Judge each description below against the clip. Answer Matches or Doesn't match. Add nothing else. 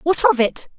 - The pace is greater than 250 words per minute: Doesn't match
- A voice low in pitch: Doesn't match